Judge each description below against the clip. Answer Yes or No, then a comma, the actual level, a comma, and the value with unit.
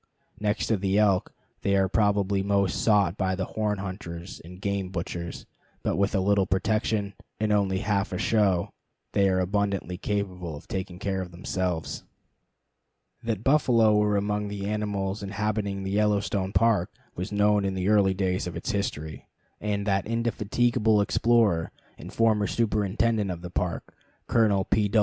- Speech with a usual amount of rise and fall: No, narrow, 2.0 semitones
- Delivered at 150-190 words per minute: Yes, average, 160 wpm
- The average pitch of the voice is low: Yes, low, 100 Hz